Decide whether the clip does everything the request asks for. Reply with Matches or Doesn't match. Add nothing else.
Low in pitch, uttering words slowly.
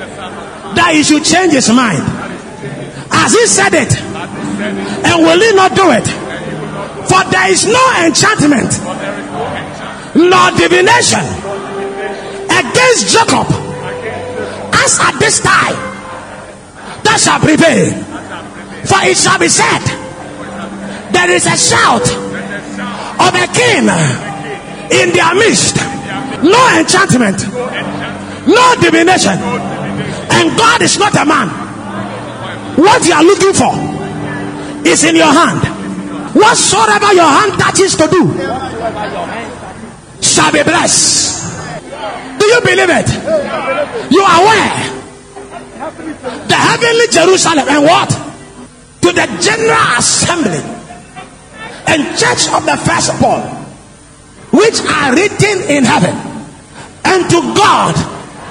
Doesn't match